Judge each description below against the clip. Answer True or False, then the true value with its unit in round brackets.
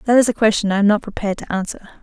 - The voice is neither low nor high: False (210 Hz)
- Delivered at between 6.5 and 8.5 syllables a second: True (7.8 syllables/s)